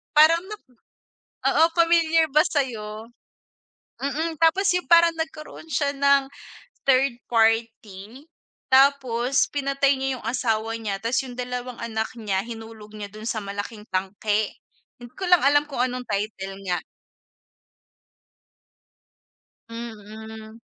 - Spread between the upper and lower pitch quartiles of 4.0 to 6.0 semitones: Yes, average, 4.5 semitones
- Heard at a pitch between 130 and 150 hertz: No, high, 245 Hz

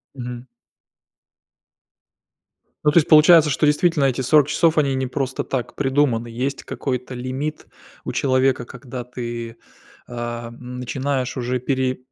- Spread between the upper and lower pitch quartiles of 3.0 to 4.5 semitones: No, narrow, 2.6 semitones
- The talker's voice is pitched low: Yes, low, 130 Hz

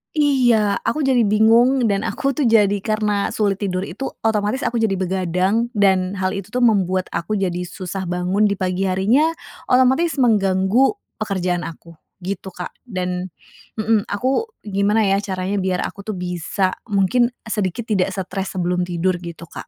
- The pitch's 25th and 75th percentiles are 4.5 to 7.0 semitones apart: No, average, 3.2 semitones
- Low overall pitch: No, high, 200 Hz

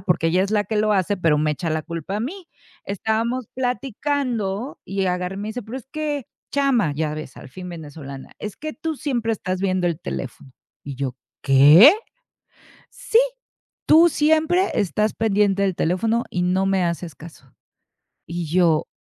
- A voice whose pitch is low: No, high, 195 Hz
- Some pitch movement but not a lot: No, wide, 6.6 semitones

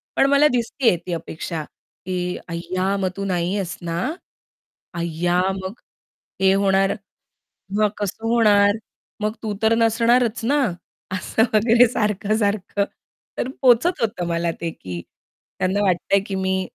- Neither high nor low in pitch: No, high, 200 Hz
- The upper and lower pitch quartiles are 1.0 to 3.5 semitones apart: No, average, 3.9 semitones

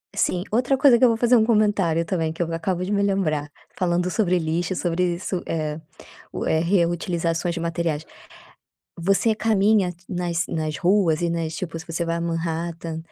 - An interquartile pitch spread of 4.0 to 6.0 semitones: No, average, 2.8 semitones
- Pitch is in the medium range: Yes, medium, 175 Hz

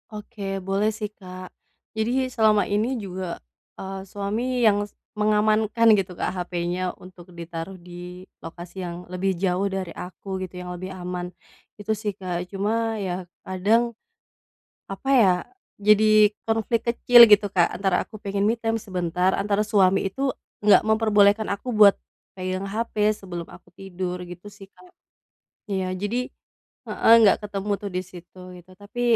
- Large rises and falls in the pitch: No, narrow, 2.6 semitones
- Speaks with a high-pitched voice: Yes, high, 195 Hz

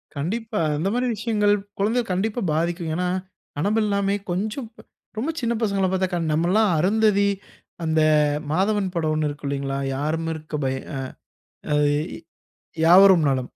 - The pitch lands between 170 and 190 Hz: Yes, medium, 185 Hz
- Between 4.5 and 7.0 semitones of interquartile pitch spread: Yes, average, 5.0 semitones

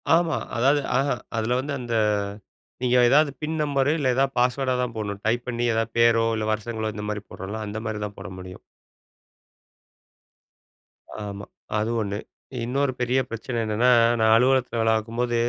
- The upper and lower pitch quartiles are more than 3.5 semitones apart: No, average, 3.1 semitones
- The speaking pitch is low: Yes, low, 120 Hz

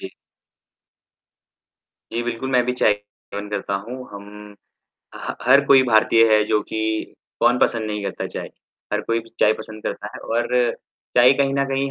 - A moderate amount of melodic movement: Yes, average, 3.1 semitones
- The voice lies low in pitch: Yes, low, 115 Hz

